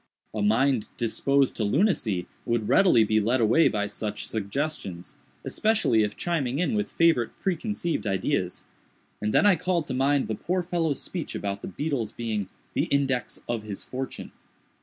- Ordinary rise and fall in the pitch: No, wide, 7.5 semitones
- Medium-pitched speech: No, low, 125 Hz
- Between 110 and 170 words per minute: Yes, average, 155 wpm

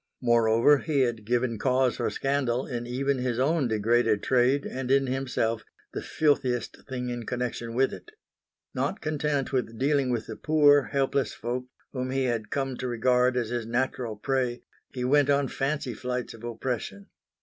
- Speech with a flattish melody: Yes, narrow, 2.3 semitones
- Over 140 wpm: Yes, average, 170 wpm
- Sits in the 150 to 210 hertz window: No, low, 125 Hz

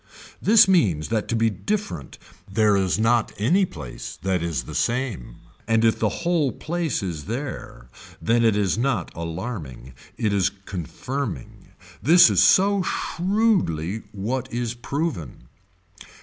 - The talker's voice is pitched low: Yes, low, 115 Hz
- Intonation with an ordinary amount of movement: No, wide, 7.6 semitones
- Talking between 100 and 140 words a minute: Yes, slow, 135 wpm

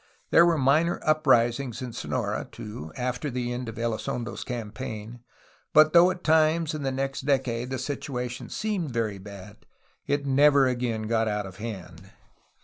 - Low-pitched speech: Yes, low, 125 Hz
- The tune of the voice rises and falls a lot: No, average, 4.3 semitones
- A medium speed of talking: Yes, average, 155 wpm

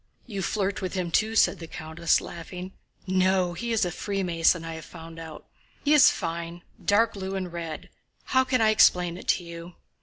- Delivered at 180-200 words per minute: Yes, average, 190 wpm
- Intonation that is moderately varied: Yes, average, 3.0 semitones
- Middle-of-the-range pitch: Yes, medium, 180 Hz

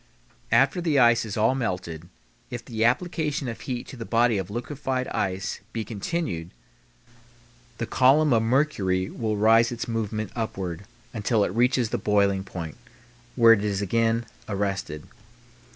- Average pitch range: Yes, average, 3.7 semitones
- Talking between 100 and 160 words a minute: Yes, average, 150 wpm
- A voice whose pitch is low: Yes, low, 115 Hz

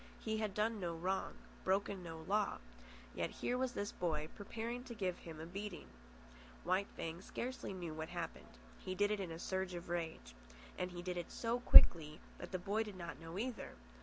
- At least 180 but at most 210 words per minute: Yes, average, 195 wpm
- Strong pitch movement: No, average, 3.7 semitones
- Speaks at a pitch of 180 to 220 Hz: Yes, medium, 185 Hz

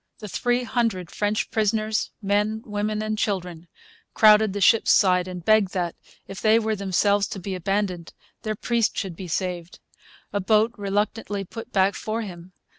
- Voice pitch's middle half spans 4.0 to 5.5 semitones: No, narrow, 2.6 semitones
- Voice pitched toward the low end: No, high, 205 Hz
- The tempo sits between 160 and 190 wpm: Yes, average, 165 wpm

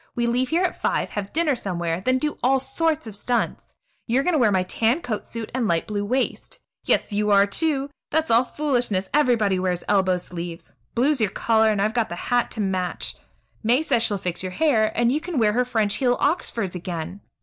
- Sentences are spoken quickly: Yes, fast, 215 wpm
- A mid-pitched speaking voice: No, high, 225 Hz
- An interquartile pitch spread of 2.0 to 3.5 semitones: No, average, 4.8 semitones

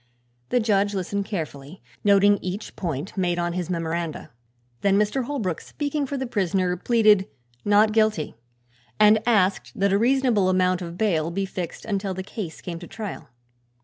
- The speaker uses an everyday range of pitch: Yes, average, 3.2 semitones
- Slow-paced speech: No, average, 160 wpm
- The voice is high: Yes, high, 195 Hz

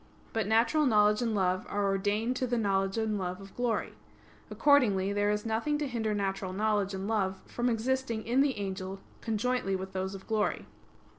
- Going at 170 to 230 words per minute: Yes, average, 180 wpm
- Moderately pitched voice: No, high, 210 Hz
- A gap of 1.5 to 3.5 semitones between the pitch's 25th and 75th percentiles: Yes, average, 3.1 semitones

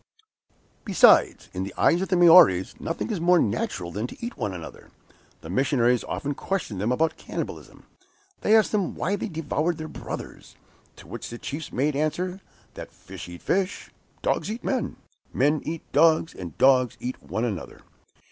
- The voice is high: No, medium, 150 Hz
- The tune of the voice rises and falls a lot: Yes, wide, 7.4 semitones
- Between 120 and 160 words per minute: No, average, 170 wpm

